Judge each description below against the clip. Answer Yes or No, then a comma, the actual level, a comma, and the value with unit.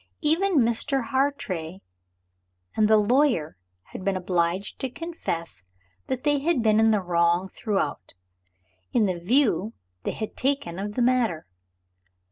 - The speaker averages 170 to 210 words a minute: No, slow, 135 wpm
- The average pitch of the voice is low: No, high, 215 Hz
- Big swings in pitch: Yes, wide, 6.7 semitones